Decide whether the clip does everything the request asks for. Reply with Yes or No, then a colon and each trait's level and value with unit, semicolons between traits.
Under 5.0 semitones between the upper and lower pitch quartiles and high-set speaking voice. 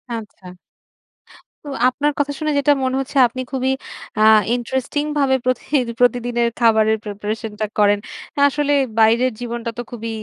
Yes: average, 3.1 semitones; high, 245 Hz